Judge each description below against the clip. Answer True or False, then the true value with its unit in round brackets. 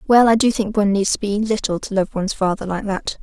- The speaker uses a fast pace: True (280 wpm)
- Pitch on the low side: False (205 Hz)